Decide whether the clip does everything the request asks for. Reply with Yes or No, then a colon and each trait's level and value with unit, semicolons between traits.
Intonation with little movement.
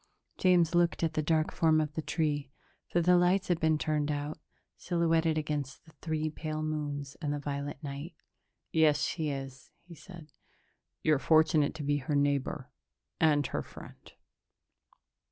Yes: narrow, 1.9 semitones